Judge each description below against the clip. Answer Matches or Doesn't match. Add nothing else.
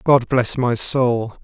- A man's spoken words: Matches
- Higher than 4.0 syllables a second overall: Doesn't match